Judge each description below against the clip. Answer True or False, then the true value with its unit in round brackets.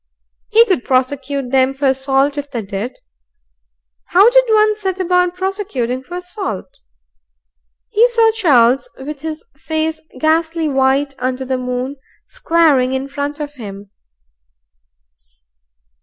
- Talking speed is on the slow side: True (125 wpm)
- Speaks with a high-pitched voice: True (285 Hz)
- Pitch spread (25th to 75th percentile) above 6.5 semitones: False (5.5 semitones)